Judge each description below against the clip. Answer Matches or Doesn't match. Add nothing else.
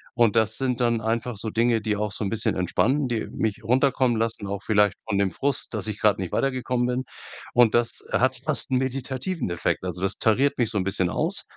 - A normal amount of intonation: Matches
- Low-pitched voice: Matches